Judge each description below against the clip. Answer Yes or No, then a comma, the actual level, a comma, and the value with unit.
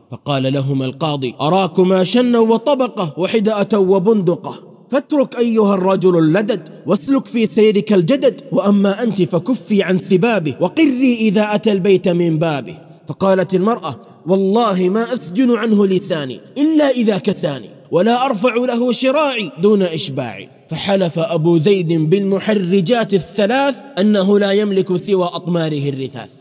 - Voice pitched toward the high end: Yes, high, 195 Hz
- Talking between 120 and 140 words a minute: Yes, average, 125 wpm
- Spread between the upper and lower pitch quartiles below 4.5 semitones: No, average, 5.0 semitones